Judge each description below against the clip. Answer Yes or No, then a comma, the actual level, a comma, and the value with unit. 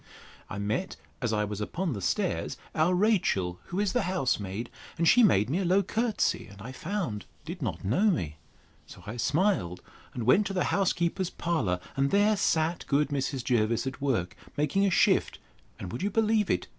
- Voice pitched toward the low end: No, medium, 150 Hz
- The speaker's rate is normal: Yes, average, 195 wpm